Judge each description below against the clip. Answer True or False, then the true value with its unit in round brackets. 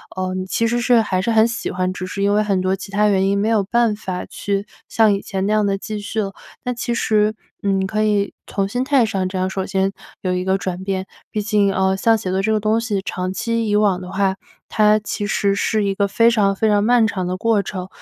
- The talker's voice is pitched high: True (200 Hz)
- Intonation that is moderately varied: False (2.2 semitones)